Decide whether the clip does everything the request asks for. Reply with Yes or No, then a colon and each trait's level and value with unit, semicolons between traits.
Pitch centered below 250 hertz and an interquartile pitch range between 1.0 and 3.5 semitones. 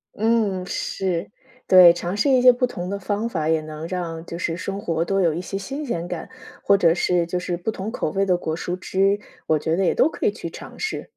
Yes: medium, 185 Hz; average, 3.1 semitones